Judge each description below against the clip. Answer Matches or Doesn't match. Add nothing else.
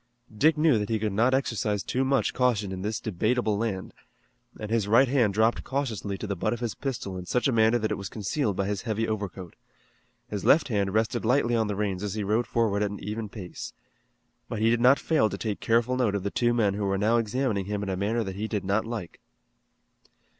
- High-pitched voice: Doesn't match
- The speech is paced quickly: Matches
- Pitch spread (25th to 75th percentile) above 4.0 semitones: Doesn't match